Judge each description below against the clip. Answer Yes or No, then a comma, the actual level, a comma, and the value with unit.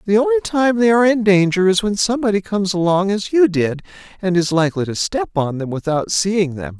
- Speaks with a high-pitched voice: Yes, high, 195 Hz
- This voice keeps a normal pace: No, fast, 220 wpm